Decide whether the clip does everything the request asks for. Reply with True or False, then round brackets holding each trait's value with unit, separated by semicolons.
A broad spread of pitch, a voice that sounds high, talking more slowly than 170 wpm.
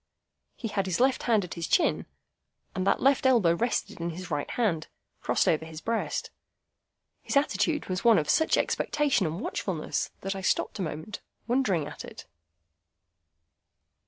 True (6.2 semitones; 195 Hz; 160 wpm)